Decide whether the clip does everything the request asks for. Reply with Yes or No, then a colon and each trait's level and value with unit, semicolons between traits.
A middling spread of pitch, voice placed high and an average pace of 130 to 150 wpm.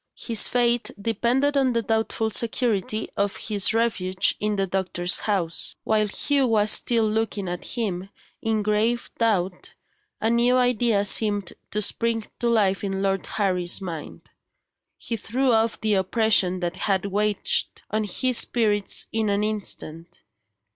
Yes: average, 3.0 semitones; high, 215 Hz; average, 145 wpm